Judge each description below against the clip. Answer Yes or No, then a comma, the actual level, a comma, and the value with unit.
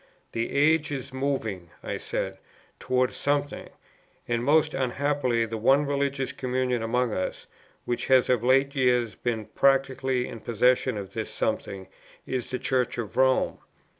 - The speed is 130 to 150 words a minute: Yes, average, 145 wpm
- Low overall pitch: Yes, low, 130 Hz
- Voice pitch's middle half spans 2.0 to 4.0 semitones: Yes, narrow, 2.5 semitones